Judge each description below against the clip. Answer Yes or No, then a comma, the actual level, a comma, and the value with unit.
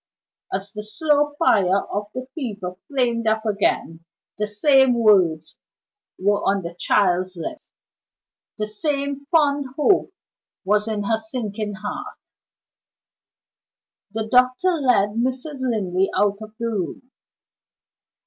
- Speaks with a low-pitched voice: No, high, 220 Hz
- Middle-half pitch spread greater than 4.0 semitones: Yes, average, 4.6 semitones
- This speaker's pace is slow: Yes, slow, 120 wpm